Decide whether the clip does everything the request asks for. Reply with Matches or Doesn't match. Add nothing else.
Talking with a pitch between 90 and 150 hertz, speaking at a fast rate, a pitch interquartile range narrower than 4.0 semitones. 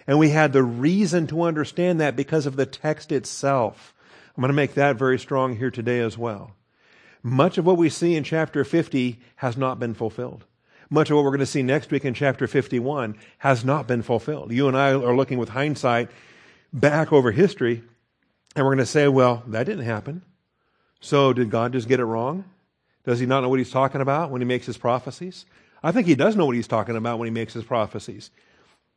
Matches